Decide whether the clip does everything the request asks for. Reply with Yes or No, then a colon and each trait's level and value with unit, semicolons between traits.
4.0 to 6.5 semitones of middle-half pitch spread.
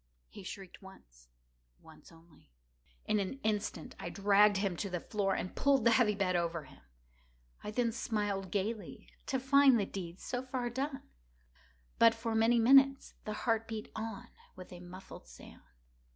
Yes: average, 4.3 semitones